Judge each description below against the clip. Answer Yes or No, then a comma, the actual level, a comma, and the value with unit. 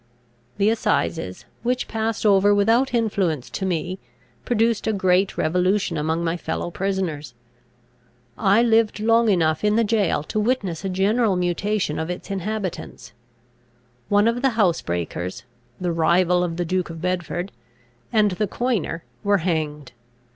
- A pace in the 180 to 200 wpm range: No, average, 140 wpm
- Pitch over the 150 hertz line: Yes, high, 190 Hz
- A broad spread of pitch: No, average, 4.3 semitones